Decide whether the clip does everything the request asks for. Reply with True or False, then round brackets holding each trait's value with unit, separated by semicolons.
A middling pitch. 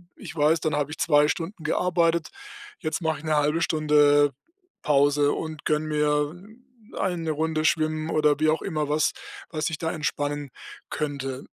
True (155 Hz)